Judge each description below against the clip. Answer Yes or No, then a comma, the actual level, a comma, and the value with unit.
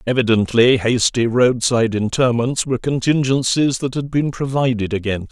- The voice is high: No, low, 125 Hz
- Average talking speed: No, slow, 125 wpm